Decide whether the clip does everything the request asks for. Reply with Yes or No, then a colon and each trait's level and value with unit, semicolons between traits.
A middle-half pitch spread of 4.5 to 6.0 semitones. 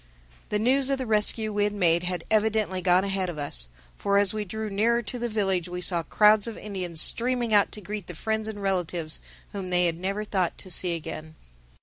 No: average, 3.4 semitones